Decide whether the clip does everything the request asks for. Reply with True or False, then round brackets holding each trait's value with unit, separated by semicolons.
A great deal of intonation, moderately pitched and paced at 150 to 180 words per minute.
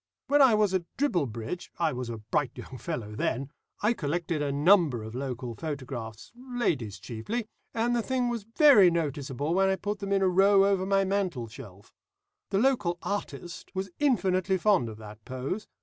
True (7.9 semitones; 175 Hz; 175 wpm)